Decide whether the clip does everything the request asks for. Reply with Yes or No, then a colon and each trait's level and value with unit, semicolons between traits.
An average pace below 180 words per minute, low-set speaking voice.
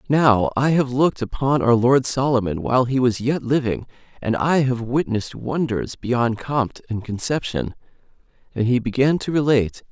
Yes: average, 165 wpm; low, 125 Hz